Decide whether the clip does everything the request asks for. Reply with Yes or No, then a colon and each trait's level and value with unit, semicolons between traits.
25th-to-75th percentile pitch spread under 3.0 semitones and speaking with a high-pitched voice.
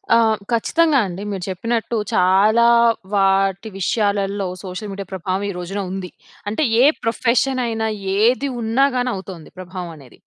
No: average, 3.6 semitones; high, 200 Hz